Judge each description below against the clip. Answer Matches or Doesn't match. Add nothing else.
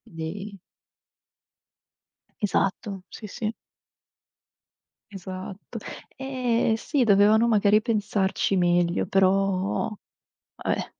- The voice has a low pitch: Doesn't match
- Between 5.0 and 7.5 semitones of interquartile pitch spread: Doesn't match